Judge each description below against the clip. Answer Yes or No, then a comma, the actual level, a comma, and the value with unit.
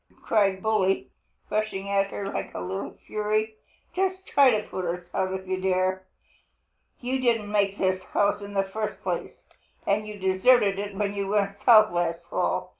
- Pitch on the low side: No, high, 200 Hz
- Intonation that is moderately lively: No, narrow, 2.1 semitones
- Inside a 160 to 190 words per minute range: Yes, average, 175 wpm